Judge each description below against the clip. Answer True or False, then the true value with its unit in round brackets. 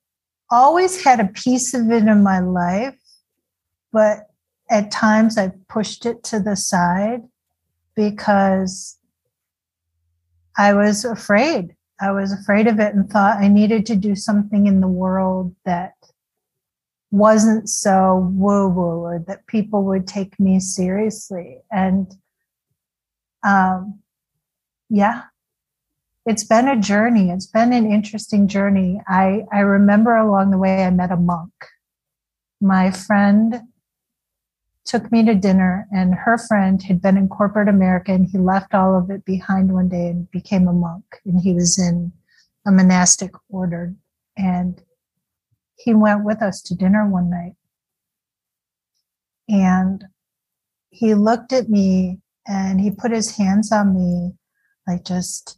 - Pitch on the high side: True (195 Hz)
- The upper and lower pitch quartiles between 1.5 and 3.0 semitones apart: True (2.5 semitones)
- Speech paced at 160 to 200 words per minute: False (135 wpm)